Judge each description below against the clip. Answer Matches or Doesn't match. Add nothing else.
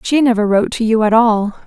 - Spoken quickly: Matches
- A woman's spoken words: Matches